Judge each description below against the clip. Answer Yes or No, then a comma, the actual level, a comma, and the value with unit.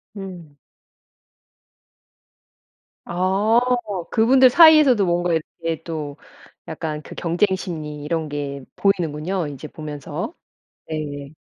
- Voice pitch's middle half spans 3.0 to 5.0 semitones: Yes, average, 4.3 semitones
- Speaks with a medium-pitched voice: Yes, medium, 165 Hz